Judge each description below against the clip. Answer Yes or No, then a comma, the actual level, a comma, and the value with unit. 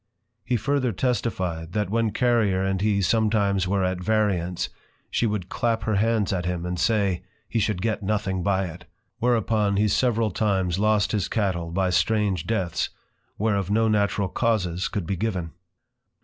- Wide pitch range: No, average, 3.2 semitones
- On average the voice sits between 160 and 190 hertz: No, low, 100 Hz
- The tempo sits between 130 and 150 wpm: No, average, 165 wpm